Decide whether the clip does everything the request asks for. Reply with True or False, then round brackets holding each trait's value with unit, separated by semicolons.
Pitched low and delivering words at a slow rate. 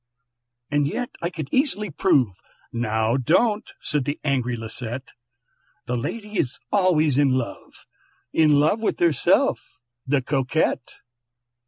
False (145 Hz; 125 wpm)